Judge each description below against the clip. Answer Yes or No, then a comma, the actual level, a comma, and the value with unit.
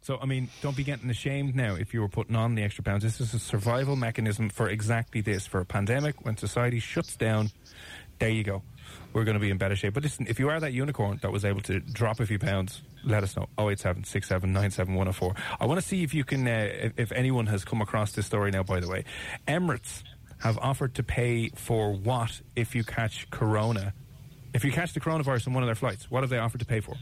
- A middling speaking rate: No, fast, 260 wpm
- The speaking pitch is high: No, low, 115 Hz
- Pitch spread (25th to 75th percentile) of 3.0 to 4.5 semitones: Yes, average, 3.8 semitones